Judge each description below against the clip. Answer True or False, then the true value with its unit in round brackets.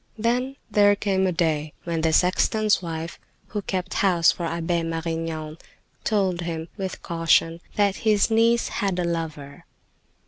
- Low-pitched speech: False (175 Hz)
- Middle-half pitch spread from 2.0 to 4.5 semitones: True (3.7 semitones)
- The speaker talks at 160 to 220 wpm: False (145 wpm)